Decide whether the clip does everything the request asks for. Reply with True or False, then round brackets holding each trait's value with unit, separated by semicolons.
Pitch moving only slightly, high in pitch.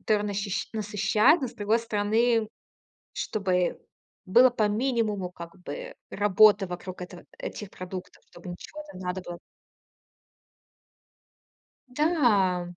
False (3.9 semitones; 205 Hz)